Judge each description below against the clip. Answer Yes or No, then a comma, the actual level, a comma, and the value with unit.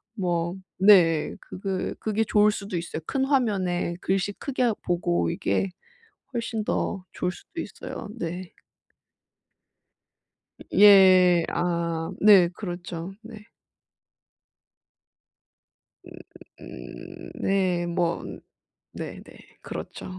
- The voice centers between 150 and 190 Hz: Yes, medium, 185 Hz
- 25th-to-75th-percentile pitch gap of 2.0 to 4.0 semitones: Yes, average, 3.2 semitones